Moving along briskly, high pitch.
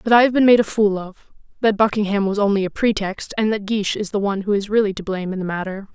Yes: fast, 285 wpm; high, 205 Hz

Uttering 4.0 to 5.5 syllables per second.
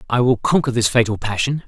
No: 6.1 syllables/s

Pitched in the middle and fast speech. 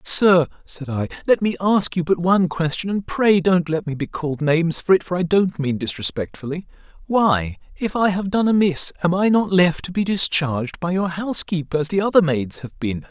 Yes: medium, 170 Hz; fast, 220 wpm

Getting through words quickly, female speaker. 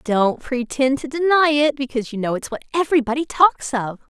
Yes: fast, 215 wpm; female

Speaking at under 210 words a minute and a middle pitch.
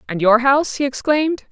No: average, 200 wpm; very high, 265 Hz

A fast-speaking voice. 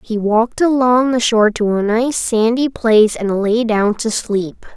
No: average, 190 wpm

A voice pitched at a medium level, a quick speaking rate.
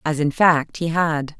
Yes: medium, 155 Hz; fast, 215 wpm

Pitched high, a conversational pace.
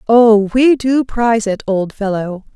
Yes: high, 220 Hz; average, 165 wpm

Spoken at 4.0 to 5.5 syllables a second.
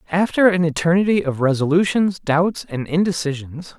Yes: 5.1 syllables/s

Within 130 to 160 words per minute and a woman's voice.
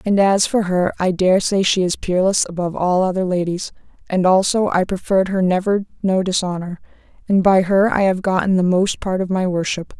No: fast, 205 wpm; female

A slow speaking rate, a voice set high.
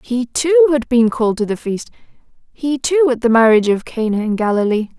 No: fast, 205 wpm; high, 245 Hz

